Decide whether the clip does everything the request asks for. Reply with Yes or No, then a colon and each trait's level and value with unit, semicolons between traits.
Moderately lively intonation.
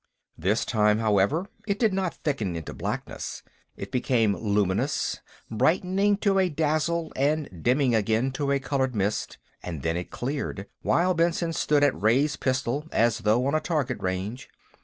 No: wide, 6.6 semitones